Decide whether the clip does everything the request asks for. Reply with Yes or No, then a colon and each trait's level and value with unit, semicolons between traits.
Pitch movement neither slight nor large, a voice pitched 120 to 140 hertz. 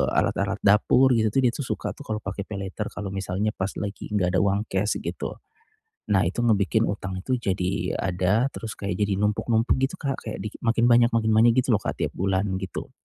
No: average, 3.0 semitones; low, 105 Hz